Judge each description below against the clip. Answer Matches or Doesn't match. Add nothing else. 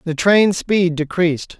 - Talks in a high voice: Doesn't match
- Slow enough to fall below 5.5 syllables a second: Matches